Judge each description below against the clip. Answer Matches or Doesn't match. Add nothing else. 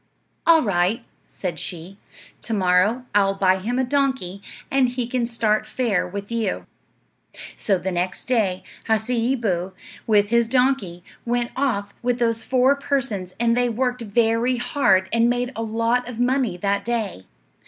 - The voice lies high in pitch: Matches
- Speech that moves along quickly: Doesn't match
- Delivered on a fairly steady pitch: Doesn't match